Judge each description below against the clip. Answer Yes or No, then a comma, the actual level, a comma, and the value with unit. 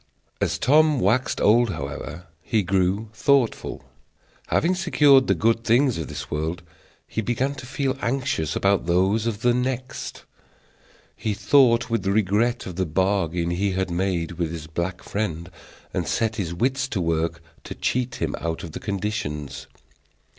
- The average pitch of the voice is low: Yes, low, 100 Hz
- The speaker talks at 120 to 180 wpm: Yes, average, 155 wpm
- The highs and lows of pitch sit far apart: Yes, wide, 6.2 semitones